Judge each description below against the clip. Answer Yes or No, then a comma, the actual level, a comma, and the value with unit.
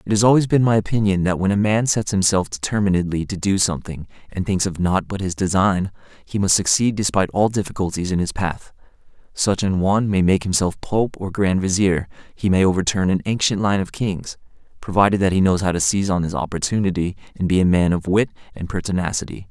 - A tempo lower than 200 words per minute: No, fast, 205 wpm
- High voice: No, very low, 95 Hz